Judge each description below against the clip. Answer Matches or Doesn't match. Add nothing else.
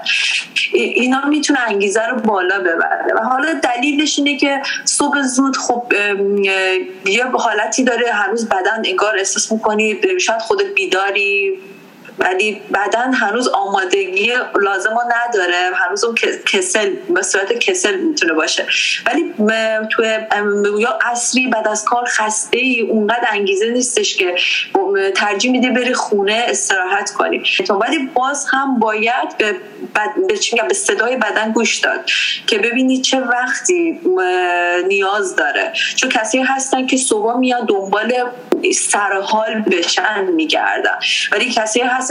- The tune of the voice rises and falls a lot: Matches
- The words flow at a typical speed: Matches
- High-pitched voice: Matches